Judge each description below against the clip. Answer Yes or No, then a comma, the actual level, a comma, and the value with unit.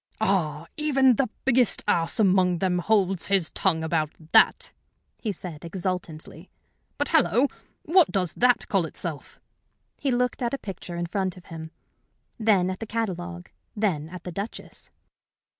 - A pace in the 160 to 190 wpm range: No, average, 150 wpm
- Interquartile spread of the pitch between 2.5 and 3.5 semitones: No, average, 4.7 semitones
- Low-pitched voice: No, high, 190 Hz